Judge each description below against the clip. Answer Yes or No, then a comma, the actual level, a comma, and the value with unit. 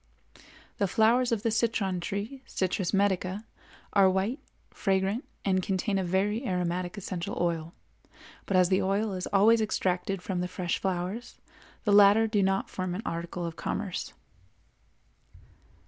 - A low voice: No, high, 195 Hz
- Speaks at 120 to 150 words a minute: Yes, average, 145 wpm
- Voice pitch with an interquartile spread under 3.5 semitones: Yes, narrow, 2.5 semitones